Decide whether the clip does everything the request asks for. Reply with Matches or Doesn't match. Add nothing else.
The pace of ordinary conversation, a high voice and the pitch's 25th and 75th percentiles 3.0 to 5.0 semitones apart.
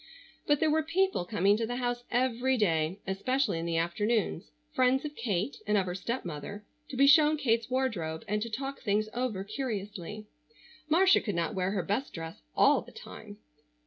Doesn't match